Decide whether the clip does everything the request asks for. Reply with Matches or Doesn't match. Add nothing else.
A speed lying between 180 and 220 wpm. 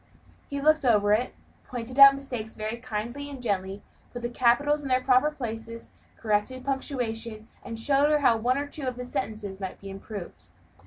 Matches